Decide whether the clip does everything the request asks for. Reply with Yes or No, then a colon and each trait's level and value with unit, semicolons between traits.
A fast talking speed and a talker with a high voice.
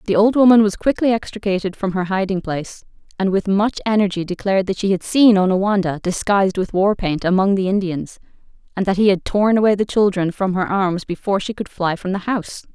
Yes: fast, 210 wpm; high, 195 Hz